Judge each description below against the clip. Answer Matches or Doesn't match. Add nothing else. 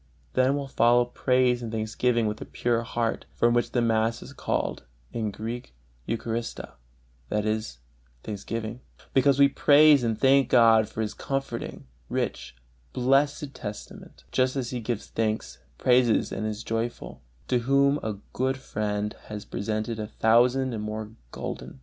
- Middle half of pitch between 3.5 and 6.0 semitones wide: Doesn't match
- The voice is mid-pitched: Doesn't match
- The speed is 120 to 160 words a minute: Matches